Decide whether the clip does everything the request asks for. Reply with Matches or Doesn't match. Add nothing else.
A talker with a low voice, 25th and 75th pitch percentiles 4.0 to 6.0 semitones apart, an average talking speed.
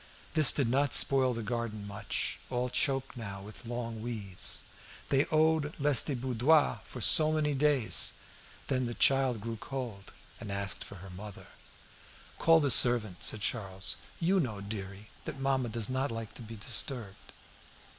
Matches